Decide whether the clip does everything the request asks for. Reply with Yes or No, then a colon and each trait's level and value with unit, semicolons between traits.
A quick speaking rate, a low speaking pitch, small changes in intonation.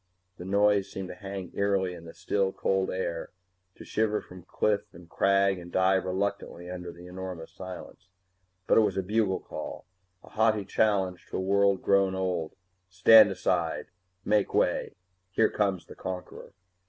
No: average, 165 wpm; very low, 95 Hz; narrow, 1.8 semitones